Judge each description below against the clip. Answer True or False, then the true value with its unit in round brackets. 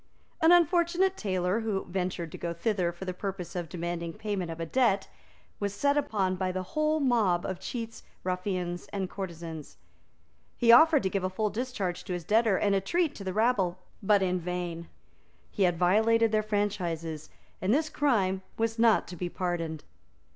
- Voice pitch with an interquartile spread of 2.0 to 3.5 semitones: False (4.2 semitones)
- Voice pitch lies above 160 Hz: True (190 Hz)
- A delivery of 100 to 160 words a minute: False (180 wpm)